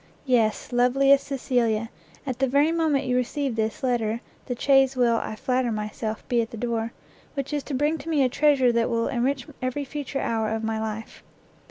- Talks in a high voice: Yes, very high, 250 Hz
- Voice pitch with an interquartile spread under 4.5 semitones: Yes, average, 3.3 semitones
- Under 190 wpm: No, average, 195 wpm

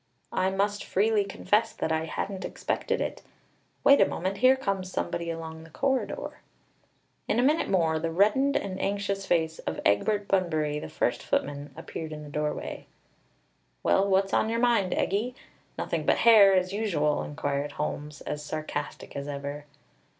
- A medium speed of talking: Yes, average, 160 wpm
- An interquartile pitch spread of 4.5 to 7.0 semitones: Yes, average, 5.2 semitones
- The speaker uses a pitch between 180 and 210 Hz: Yes, medium, 185 Hz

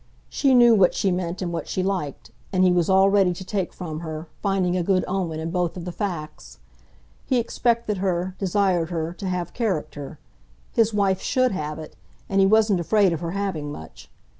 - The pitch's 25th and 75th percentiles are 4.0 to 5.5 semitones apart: No, average, 2.9 semitones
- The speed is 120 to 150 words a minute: No, average, 200 wpm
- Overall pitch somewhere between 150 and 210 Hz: Yes, medium, 185 Hz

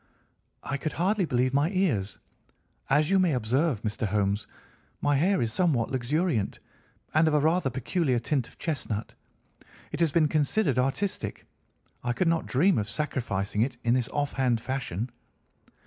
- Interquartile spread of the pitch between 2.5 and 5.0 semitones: No, wide, 5.4 semitones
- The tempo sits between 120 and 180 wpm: Yes, average, 155 wpm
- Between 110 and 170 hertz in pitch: Yes, low, 135 Hz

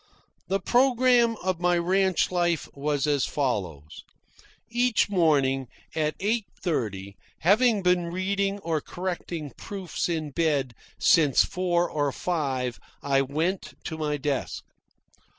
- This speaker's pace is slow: Yes, slow, 120 wpm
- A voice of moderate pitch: Yes, medium, 170 Hz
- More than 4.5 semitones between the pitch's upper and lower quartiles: Yes, average, 5.0 semitones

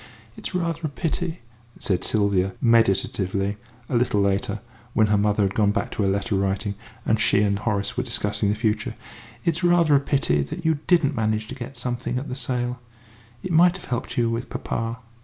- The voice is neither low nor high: No, low, 115 Hz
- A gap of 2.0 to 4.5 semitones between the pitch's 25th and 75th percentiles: No, average, 5.2 semitones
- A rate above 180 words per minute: Yes, average, 195 wpm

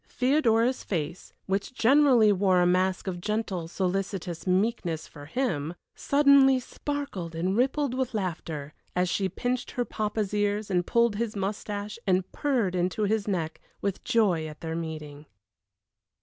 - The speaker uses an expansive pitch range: No, average, 4.8 semitones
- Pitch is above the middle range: Yes, high, 200 Hz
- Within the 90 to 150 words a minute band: Yes, average, 145 wpm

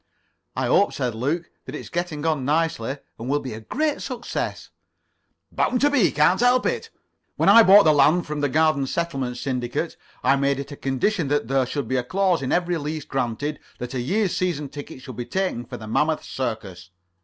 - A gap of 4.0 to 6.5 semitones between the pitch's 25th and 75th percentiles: Yes, average, 5.1 semitones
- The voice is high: No, medium, 145 Hz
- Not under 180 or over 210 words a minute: Yes, average, 200 wpm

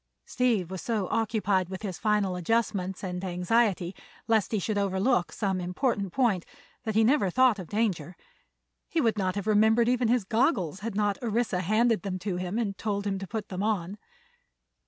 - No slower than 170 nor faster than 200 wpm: Yes, average, 180 wpm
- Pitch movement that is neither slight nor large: Yes, average, 3.4 semitones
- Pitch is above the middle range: Yes, high, 205 Hz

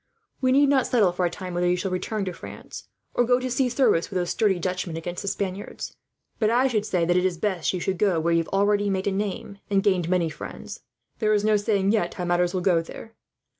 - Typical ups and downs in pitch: Yes, average, 3.2 semitones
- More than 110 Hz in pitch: Yes, high, 190 Hz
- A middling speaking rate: No, fast, 250 wpm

